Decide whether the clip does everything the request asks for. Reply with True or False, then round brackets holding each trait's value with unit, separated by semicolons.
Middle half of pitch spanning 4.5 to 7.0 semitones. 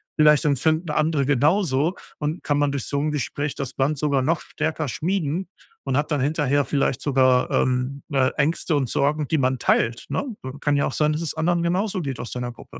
False (2.8 semitones)